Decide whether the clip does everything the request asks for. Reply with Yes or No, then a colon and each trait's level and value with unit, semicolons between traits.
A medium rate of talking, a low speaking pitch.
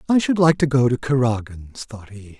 No: fast, 225 wpm; low, 125 Hz